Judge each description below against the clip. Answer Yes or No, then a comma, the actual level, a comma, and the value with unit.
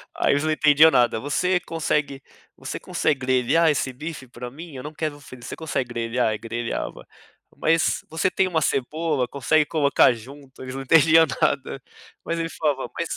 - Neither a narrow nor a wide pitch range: Yes, average, 3.8 semitones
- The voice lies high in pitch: No, medium, 145 Hz